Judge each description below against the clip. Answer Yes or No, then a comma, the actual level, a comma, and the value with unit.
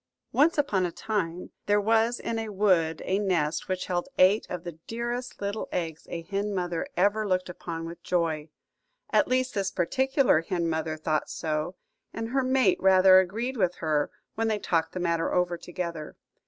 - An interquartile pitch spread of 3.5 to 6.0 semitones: Yes, average, 4.5 semitones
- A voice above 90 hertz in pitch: Yes, medium, 185 Hz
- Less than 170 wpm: No, average, 180 wpm